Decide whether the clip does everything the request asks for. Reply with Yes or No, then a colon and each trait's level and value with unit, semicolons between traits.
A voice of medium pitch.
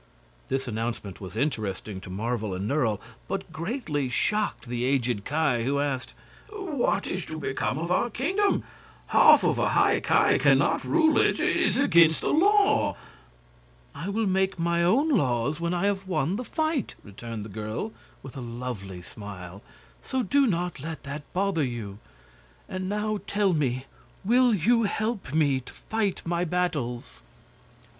Yes: medium, 155 Hz